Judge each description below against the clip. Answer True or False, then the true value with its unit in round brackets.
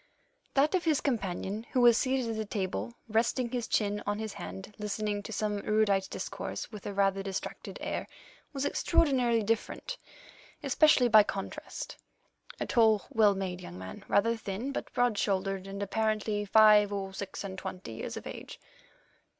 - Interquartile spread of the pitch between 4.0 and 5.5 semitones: False (2.9 semitones)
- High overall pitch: True (210 Hz)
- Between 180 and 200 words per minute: False (165 wpm)